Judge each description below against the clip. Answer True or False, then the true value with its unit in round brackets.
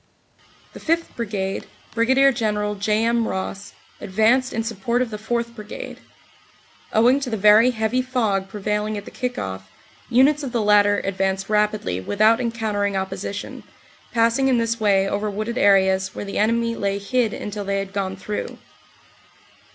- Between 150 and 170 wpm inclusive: True (160 wpm)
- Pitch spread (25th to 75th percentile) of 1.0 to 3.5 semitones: True (2.8 semitones)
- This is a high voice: True (215 Hz)